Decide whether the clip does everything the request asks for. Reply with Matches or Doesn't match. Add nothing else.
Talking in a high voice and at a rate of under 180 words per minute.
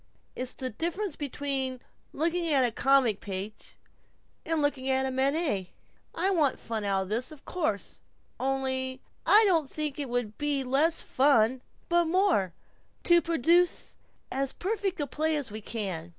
Matches